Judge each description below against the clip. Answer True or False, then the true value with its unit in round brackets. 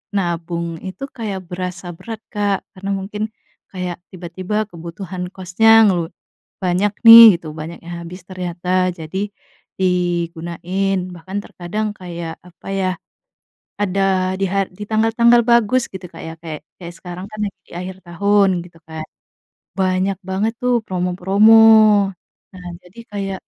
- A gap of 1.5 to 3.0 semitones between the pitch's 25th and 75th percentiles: True (2.5 semitones)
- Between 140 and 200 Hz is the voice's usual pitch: True (185 Hz)